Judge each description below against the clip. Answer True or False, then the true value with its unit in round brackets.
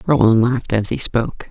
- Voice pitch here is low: True (115 Hz)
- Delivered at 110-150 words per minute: False (200 wpm)